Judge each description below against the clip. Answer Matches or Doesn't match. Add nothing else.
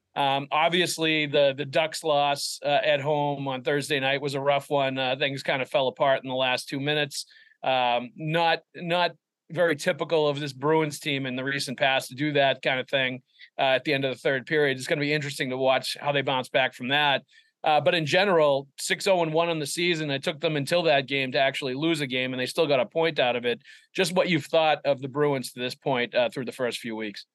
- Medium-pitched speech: Matches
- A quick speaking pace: Matches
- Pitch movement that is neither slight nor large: Matches